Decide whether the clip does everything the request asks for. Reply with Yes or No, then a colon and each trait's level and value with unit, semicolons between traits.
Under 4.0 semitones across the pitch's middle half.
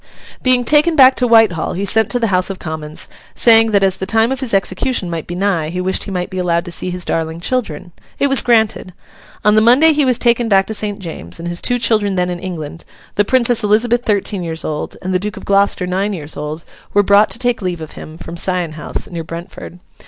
No: average, 4.6 semitones